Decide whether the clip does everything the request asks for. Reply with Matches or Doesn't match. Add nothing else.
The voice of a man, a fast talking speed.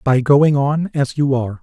Matches